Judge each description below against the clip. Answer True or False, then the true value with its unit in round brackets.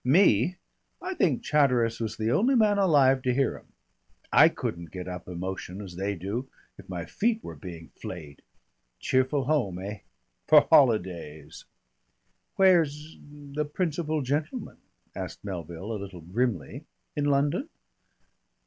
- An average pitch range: False (8.2 semitones)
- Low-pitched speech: True (125 Hz)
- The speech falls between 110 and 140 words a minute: True (135 wpm)